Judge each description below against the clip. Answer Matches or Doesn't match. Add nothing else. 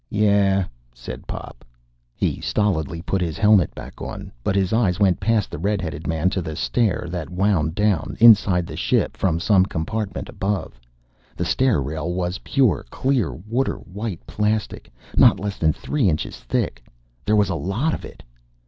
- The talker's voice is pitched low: Matches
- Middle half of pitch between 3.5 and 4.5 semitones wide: Matches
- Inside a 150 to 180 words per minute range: Matches